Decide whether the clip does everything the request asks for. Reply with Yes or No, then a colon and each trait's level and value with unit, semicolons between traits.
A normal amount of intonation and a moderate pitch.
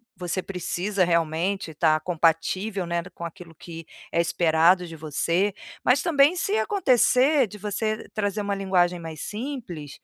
Yes: average, 4.0 semitones; medium, 180 Hz